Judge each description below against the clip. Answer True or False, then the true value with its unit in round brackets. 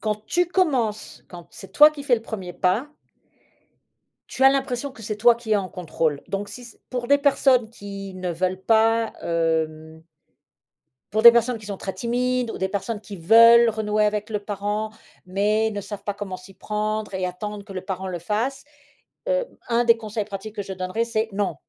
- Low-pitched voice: False (210 Hz)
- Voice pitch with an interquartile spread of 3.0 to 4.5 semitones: True (3.4 semitones)